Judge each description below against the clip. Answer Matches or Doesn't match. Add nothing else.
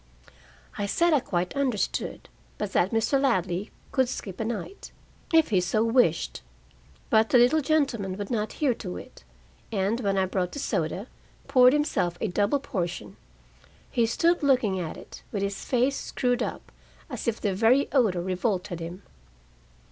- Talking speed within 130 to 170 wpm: Matches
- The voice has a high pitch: Matches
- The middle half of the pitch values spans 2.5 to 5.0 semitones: Doesn't match